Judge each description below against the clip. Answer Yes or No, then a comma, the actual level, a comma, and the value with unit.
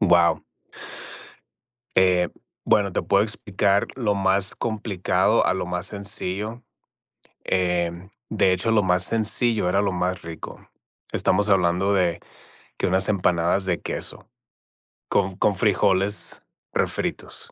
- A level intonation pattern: Yes, narrow, 2.3 semitones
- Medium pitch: No, very low, 95 Hz